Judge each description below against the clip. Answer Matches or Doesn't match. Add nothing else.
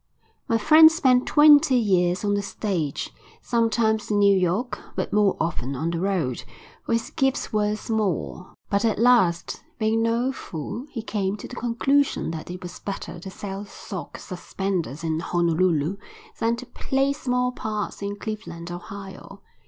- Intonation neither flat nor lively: Matches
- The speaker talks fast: Doesn't match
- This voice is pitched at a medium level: Doesn't match